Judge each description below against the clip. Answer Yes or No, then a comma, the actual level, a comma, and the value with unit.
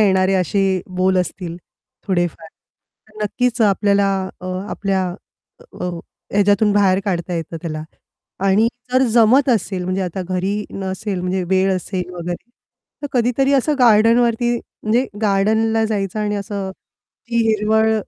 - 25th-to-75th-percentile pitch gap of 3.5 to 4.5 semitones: No, average, 2.9 semitones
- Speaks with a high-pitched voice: Yes, high, 200 Hz